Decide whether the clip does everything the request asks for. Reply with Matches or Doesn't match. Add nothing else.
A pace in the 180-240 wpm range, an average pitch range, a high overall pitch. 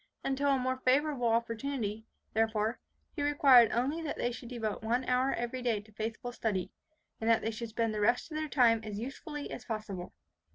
Matches